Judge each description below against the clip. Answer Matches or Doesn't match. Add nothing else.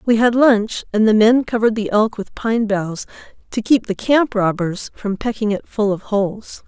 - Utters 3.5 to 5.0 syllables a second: Matches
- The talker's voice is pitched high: Matches